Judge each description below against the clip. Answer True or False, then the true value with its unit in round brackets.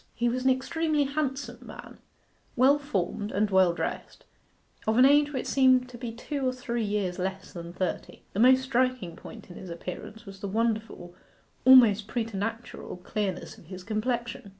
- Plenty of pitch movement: False (4.9 semitones)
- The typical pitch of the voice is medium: False (230 Hz)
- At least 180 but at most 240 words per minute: False (170 wpm)